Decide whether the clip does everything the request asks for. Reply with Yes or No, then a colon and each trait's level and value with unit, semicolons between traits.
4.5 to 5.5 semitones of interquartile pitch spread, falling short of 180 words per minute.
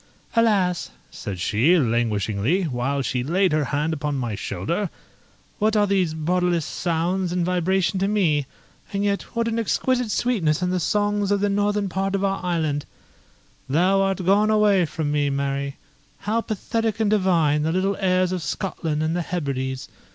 Yes: average, 5.0 semitones; average, 165 wpm